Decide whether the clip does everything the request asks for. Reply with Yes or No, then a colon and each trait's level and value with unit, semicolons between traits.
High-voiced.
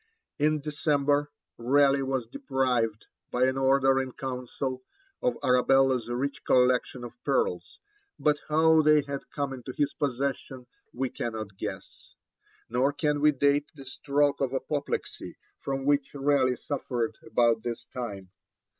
No: low, 135 Hz